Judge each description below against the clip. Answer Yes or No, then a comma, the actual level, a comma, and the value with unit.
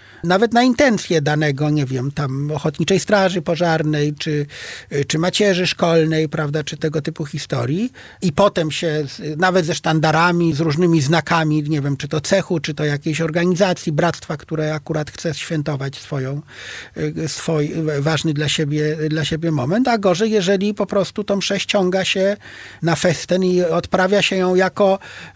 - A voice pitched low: No, medium, 165 Hz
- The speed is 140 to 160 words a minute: Yes, average, 155 wpm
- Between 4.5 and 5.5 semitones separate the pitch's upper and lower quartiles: No, average, 3.3 semitones